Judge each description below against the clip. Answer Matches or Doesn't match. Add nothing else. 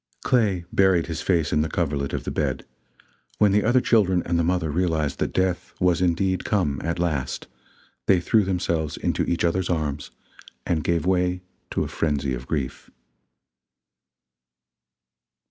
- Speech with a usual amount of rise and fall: Matches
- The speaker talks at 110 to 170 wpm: Matches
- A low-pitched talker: Matches